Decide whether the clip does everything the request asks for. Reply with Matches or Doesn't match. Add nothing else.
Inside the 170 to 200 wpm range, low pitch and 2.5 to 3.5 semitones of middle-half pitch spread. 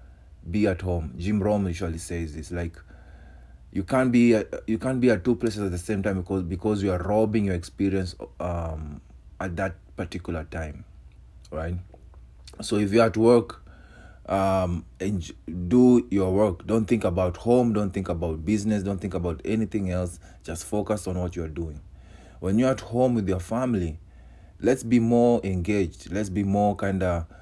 Doesn't match